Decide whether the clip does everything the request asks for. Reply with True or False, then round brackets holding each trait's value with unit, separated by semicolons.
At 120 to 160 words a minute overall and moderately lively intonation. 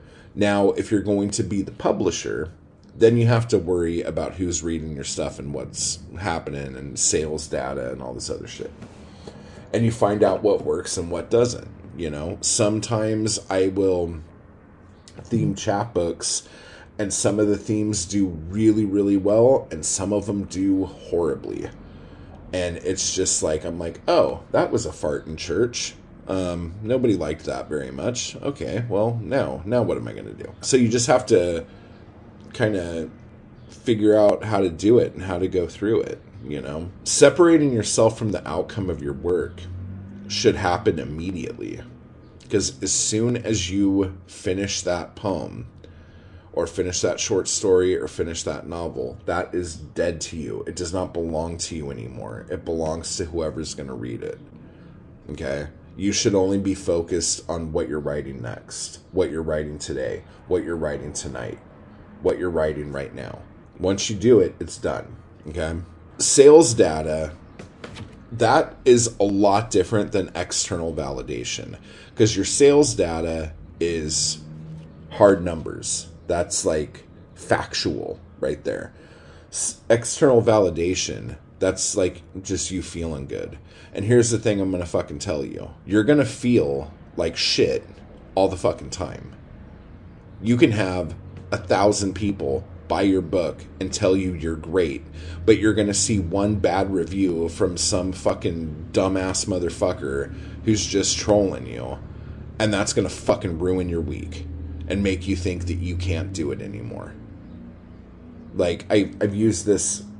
True (155 wpm; 4.0 semitones)